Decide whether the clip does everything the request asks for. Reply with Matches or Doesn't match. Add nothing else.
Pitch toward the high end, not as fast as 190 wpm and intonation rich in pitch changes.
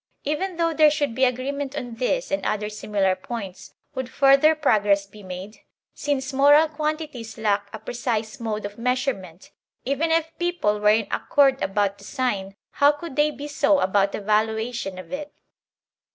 Matches